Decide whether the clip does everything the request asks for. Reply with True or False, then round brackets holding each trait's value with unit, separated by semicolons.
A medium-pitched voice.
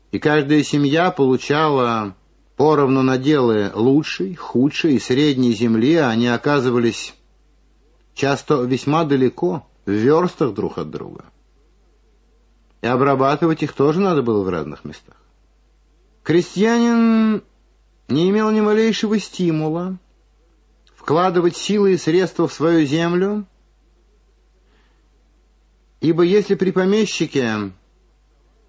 True (155 Hz)